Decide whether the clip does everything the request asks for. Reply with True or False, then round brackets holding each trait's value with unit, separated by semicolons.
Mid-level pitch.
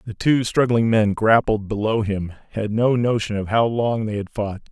False (110 Hz)